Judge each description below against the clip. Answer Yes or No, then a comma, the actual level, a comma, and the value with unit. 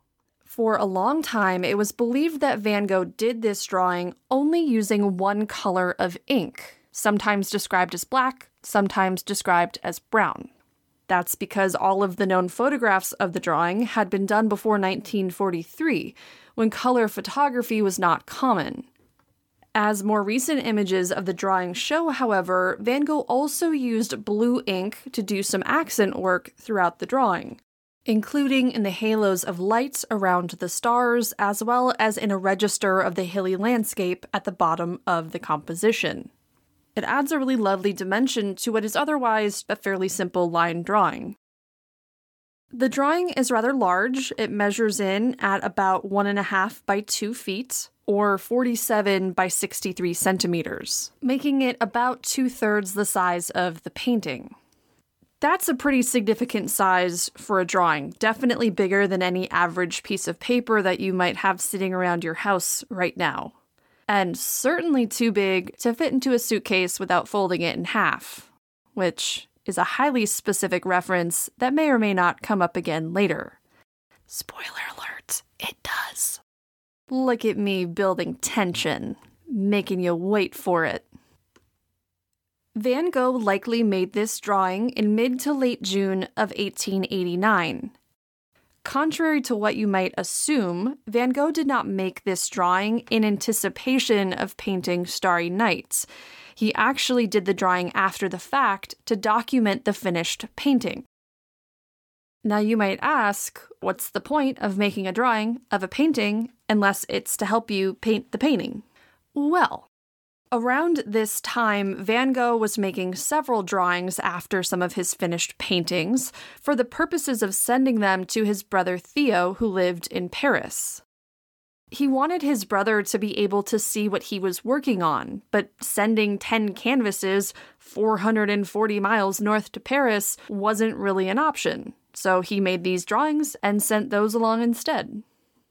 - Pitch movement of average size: Yes, average, 4.3 semitones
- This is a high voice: Yes, high, 210 Hz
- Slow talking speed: No, average, 155 wpm